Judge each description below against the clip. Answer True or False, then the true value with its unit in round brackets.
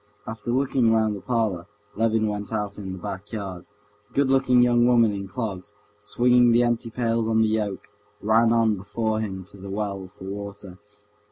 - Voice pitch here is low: True (110 Hz)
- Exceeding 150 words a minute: True (185 wpm)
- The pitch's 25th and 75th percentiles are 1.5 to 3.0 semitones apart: True (2.7 semitones)